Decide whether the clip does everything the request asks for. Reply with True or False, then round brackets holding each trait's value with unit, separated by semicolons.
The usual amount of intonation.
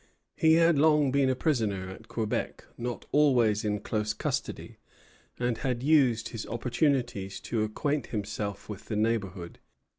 True (4.7 semitones)